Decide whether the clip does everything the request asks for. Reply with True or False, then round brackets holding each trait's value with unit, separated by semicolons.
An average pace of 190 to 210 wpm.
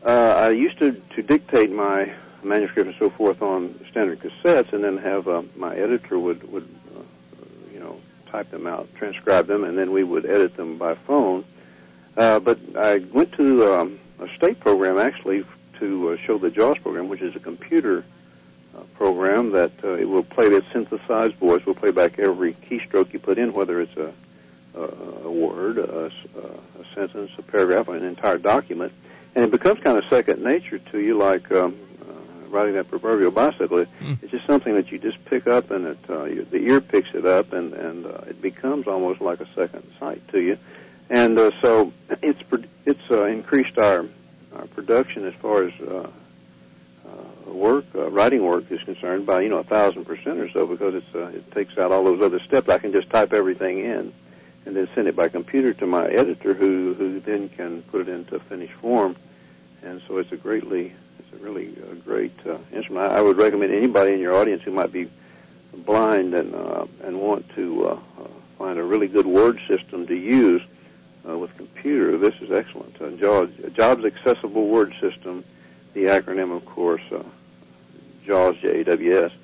True (195 wpm)